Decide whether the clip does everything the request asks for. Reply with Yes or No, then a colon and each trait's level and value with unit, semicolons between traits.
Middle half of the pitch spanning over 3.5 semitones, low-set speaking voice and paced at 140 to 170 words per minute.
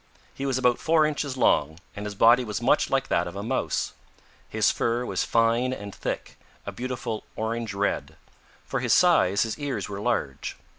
No: average, 3.9 semitones; low, 115 Hz; average, 185 wpm